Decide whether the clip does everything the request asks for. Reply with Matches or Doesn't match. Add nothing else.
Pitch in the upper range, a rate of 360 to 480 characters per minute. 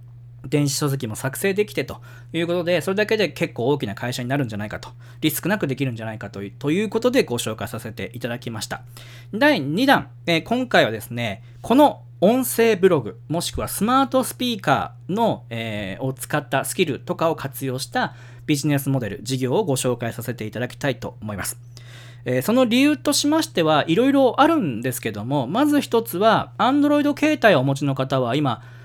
Doesn't match